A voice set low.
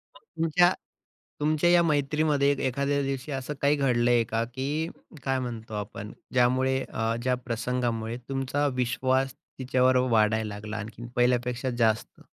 Yes: low, 125 Hz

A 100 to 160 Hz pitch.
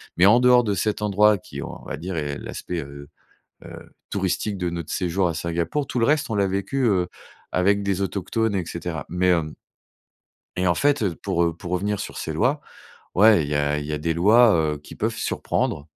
No: very low, 90 Hz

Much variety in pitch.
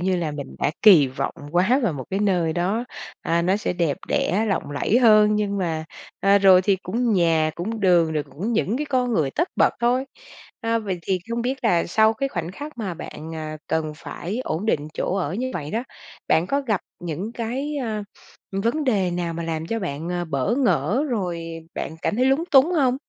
Yes: wide, 5.8 semitones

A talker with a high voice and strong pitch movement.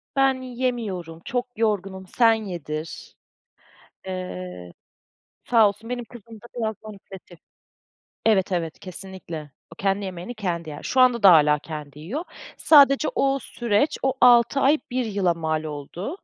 Yes: high, 200 Hz; wide, 6.3 semitones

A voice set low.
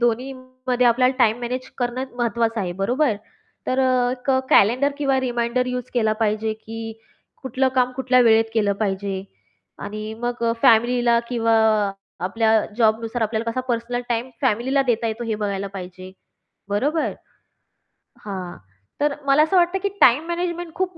No: high, 240 Hz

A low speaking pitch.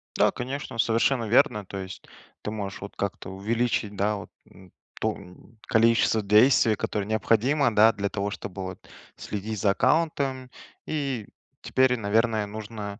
Yes: low, 110 Hz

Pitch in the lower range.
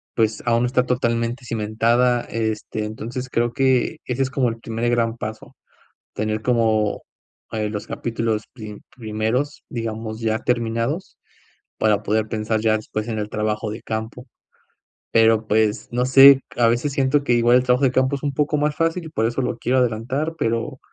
Yes: low, 115 Hz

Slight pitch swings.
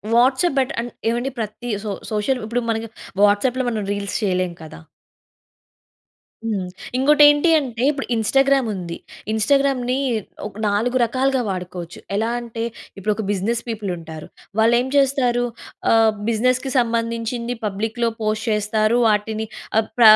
No: average, 3.2 semitones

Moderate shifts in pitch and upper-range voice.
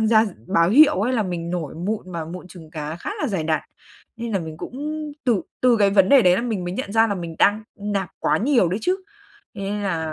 Yes: average, 4.8 semitones; high, 200 Hz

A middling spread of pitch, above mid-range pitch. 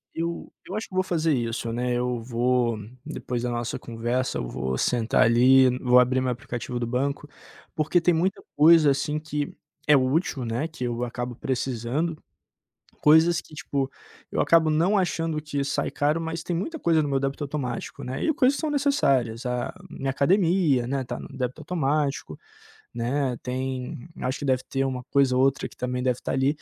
No: average, 4.2 semitones; low, 135 Hz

